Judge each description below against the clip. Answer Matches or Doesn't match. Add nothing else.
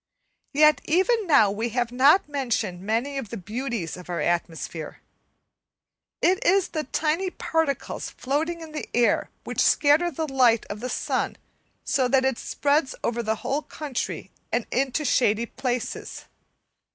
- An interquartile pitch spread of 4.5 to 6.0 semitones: Matches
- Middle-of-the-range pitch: Doesn't match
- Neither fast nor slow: Matches